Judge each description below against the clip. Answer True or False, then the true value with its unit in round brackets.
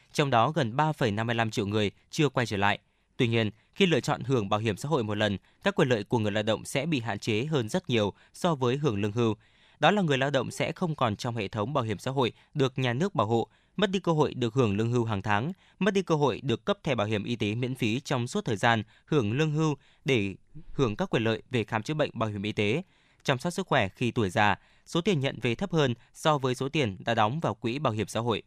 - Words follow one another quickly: True (270 wpm)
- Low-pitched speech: True (125 Hz)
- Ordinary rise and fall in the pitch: False (5.7 semitones)